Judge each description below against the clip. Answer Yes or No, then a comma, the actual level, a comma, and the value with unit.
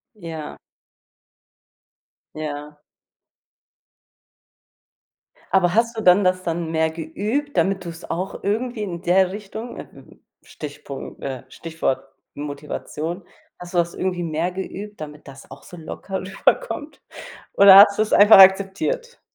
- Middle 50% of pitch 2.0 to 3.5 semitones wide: No, average, 4.0 semitones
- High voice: No, medium, 180 Hz